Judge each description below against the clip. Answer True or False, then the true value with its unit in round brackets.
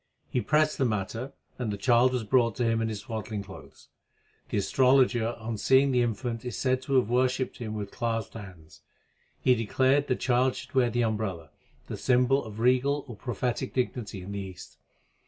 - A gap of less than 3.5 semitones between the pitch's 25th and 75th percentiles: True (3.0 semitones)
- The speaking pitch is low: True (120 Hz)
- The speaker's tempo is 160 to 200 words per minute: True (190 wpm)